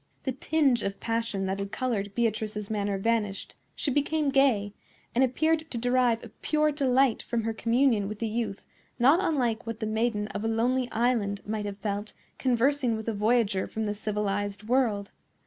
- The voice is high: Yes, high, 230 Hz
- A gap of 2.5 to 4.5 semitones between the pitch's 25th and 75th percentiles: Yes, average, 3.6 semitones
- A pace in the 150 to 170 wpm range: No, average, 180 wpm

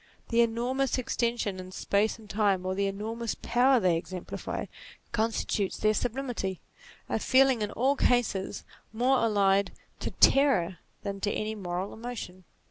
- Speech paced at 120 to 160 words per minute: Yes, average, 140 wpm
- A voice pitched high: Yes, high, 215 Hz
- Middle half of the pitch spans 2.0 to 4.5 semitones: Yes, average, 3.9 semitones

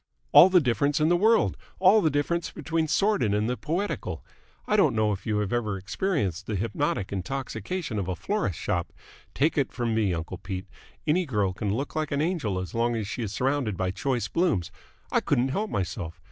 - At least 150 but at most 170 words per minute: No, average, 200 wpm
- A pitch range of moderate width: No, wide, 8.0 semitones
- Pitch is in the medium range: No, low, 120 Hz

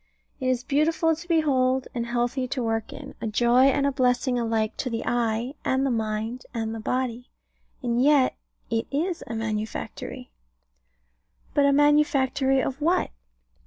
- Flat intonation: No, average, 3.4 semitones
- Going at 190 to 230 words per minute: No, average, 155 wpm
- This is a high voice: Yes, very high, 255 Hz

